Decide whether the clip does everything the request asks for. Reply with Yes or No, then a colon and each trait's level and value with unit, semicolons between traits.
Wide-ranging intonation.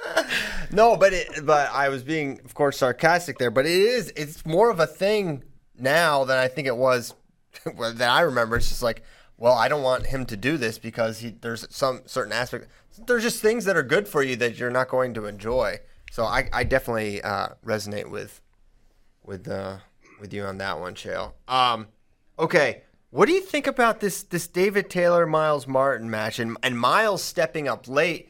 Yes: wide, 7.2 semitones